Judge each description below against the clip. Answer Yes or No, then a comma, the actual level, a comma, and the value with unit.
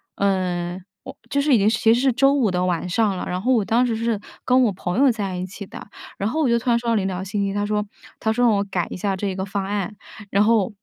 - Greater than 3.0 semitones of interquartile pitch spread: Yes, average, 3.5 semitones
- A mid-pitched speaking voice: No, high, 205 Hz